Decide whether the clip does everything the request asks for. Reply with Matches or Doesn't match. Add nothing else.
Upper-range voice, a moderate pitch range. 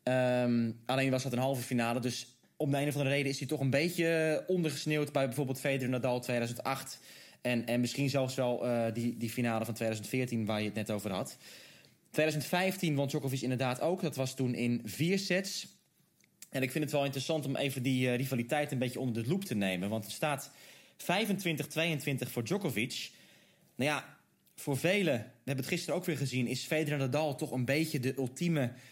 Doesn't match